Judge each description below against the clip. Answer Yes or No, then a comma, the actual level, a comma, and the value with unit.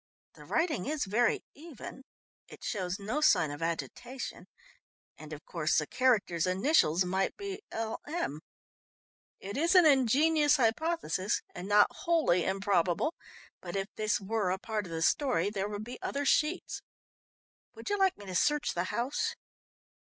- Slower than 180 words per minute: Yes, average, 150 wpm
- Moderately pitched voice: No, high, 215 Hz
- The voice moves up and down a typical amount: No, wide, 8.1 semitones